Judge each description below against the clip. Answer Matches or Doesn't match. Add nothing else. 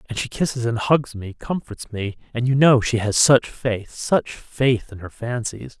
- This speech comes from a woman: Doesn't match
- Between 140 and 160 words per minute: Doesn't match